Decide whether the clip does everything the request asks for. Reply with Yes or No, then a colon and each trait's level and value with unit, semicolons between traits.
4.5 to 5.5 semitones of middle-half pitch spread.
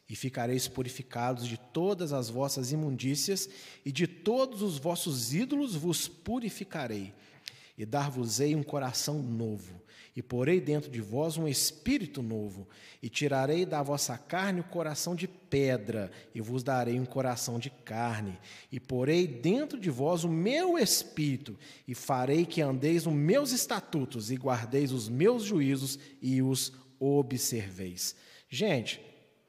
Yes: average, 5.2 semitones